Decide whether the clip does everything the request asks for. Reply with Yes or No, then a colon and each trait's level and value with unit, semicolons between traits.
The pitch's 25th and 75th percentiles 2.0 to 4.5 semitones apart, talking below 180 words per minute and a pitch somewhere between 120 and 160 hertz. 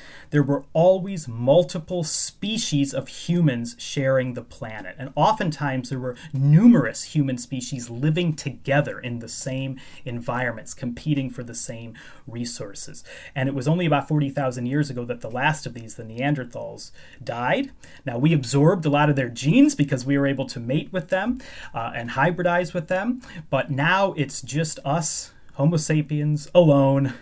Yes: average, 3.9 semitones; average, 160 wpm; medium, 140 Hz